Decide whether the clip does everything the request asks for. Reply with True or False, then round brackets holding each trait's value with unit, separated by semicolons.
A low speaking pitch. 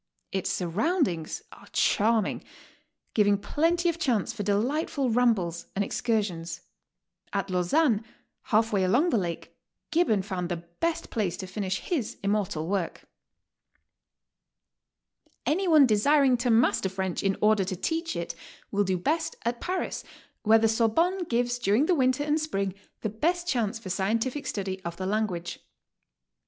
False (220 Hz)